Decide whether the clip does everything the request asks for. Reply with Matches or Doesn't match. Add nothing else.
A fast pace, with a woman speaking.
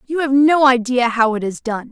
Matches